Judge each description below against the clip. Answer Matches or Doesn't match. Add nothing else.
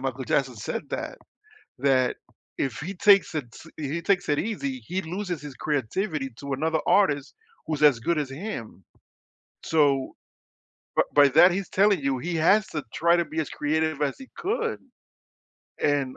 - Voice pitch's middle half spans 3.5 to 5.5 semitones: Matches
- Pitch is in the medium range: Matches